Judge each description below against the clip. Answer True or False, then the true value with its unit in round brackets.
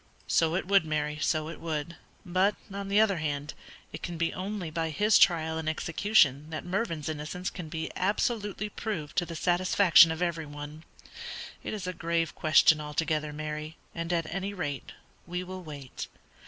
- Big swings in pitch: False (3.3 semitones)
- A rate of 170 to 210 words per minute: True (175 wpm)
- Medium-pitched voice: True (165 Hz)